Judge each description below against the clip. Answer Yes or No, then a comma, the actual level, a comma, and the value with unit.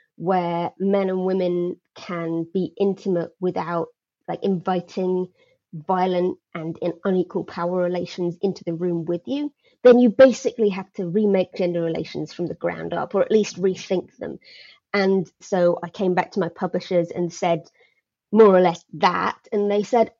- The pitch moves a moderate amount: No, narrow, 2.3 semitones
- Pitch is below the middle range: No, medium, 185 Hz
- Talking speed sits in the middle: Yes, average, 165 wpm